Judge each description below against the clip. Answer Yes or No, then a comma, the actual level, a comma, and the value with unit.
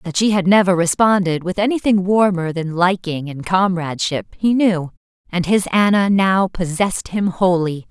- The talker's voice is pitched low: No, medium, 185 Hz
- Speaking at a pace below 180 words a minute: Yes, average, 160 wpm